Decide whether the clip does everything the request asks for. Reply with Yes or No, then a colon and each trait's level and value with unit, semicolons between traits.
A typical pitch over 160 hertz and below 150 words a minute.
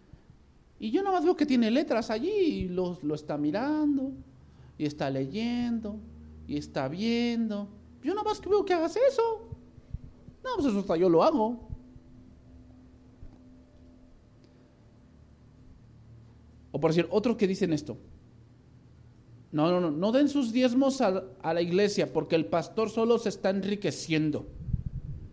Yes: high, 190 Hz; average, 140 wpm